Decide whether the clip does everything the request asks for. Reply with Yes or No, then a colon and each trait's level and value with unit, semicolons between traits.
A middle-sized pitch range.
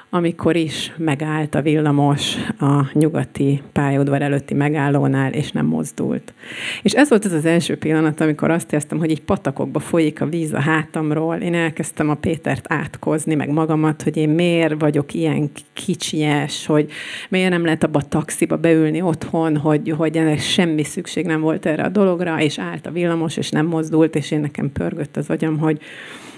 No: narrow, 1.7 semitones